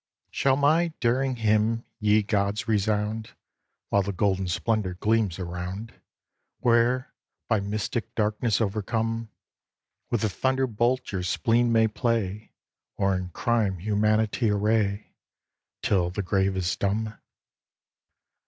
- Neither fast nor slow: No, slow, 115 wpm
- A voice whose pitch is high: No, low, 110 Hz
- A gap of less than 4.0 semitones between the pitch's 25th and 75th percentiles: Yes, average, 2.7 semitones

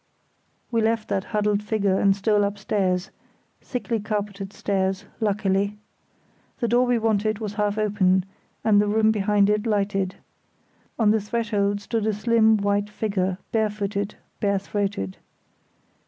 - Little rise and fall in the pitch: Yes, narrow, 1.6 semitones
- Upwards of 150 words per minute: No, slow, 135 wpm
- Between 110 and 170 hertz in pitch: No, high, 205 Hz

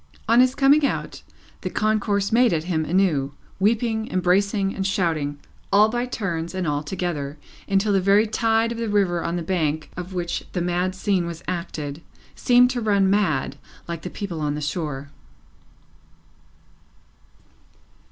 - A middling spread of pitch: Yes, average, 4.4 semitones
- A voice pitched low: No, medium, 185 Hz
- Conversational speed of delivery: Yes, average, 155 wpm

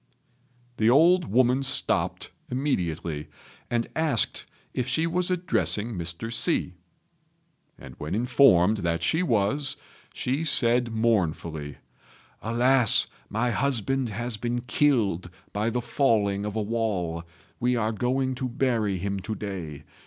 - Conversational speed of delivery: No, slow, 125 wpm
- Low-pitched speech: Yes, low, 115 Hz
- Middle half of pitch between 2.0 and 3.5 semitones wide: No, average, 4.6 semitones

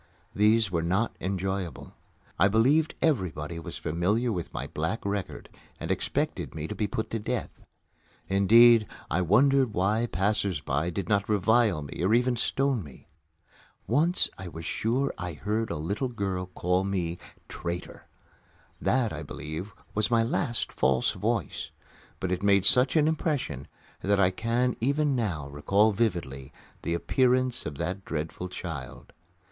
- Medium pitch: No, low, 100 Hz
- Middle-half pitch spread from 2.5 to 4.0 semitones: No, average, 5.3 semitones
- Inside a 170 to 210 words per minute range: No, average, 150 wpm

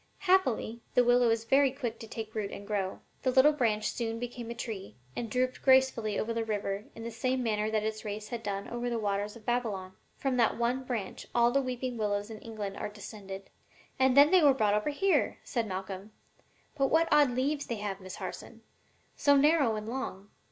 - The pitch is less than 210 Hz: No, high, 230 Hz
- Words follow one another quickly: Yes, fast, 210 wpm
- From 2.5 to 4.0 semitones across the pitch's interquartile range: Yes, average, 3.5 semitones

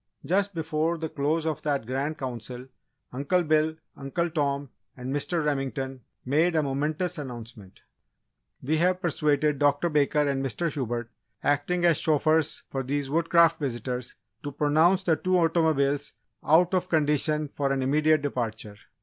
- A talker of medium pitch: Yes, medium, 150 Hz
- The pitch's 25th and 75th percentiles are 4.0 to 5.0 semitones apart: No, average, 3.1 semitones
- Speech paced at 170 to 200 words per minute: No, average, 145 wpm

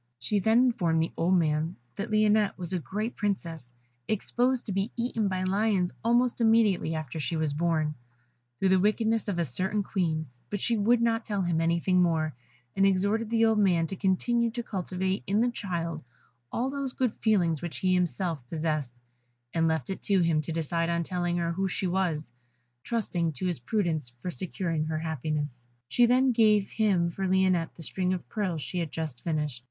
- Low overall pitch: No, medium, 185 Hz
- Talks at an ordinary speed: Yes, average, 190 wpm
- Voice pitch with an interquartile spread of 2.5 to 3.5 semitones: No, average, 4.6 semitones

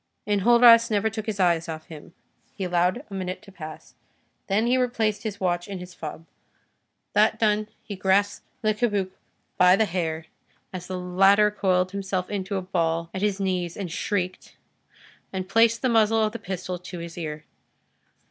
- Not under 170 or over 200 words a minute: Yes, average, 175 wpm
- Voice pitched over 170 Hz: Yes, high, 190 Hz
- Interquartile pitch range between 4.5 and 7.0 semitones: No, average, 3.0 semitones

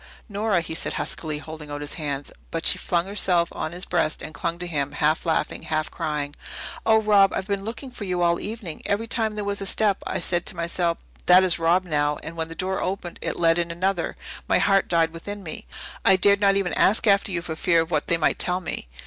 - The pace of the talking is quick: Yes, fast, 240 wpm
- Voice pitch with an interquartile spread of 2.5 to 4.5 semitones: Yes, average, 3.4 semitones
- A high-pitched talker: No, medium, 175 Hz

